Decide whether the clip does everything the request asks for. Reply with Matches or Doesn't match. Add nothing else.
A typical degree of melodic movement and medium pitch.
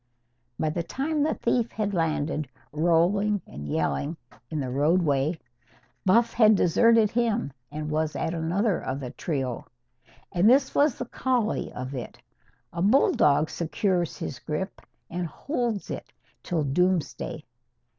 Doesn't match